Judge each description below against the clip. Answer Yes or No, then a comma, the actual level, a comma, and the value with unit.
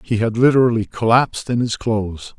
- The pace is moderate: Yes, average, 175 wpm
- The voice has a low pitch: Yes, low, 115 Hz